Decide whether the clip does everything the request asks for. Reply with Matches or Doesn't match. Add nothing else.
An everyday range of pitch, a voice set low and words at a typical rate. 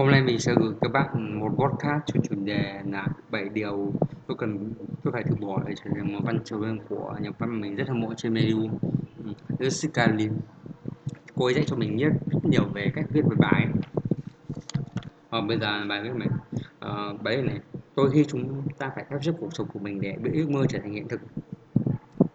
Matches